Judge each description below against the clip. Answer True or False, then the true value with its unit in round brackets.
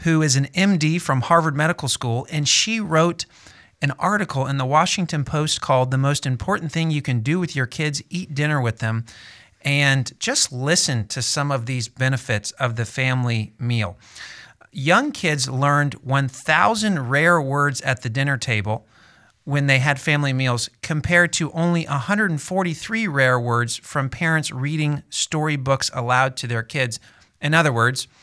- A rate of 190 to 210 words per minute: False (160 wpm)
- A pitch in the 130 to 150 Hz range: True (140 Hz)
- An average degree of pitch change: True (4.0 semitones)